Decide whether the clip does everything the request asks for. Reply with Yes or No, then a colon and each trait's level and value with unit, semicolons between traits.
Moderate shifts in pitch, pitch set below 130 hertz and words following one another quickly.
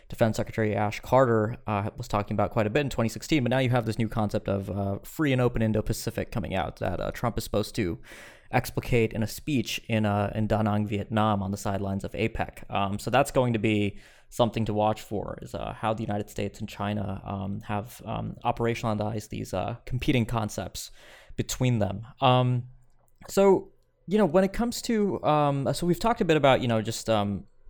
Yes: average, 3.3 semitones; low, 110 Hz; fast, 210 wpm